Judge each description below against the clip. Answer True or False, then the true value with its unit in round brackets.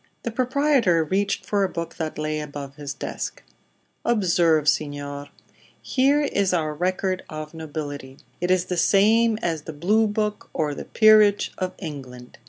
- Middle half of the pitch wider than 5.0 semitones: True (5.5 semitones)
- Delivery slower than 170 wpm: True (155 wpm)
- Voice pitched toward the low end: False (175 Hz)